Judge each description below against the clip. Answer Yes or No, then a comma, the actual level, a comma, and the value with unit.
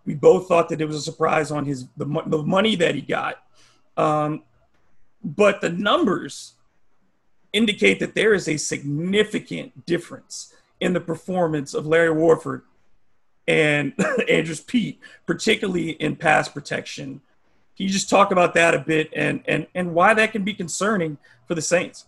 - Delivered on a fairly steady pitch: No, average, 3.7 semitones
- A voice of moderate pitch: Yes, medium, 165 Hz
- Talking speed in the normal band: Yes, average, 165 wpm